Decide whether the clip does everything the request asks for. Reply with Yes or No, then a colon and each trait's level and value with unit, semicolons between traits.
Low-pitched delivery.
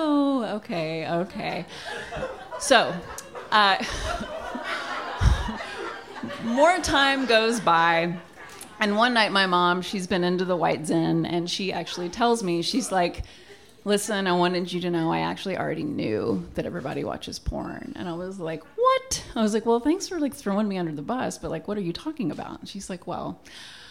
No: high, 195 Hz